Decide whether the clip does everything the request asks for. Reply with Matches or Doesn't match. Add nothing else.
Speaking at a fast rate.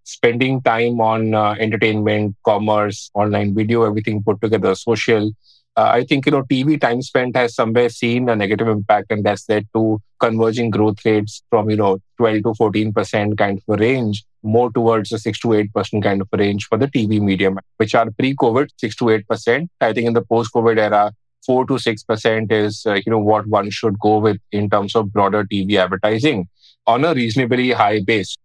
Doesn't match